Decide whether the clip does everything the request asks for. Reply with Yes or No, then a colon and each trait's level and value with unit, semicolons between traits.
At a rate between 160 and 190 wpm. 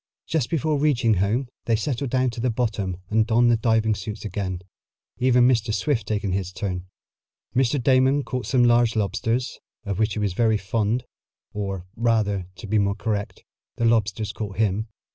Yes: average, 175 wpm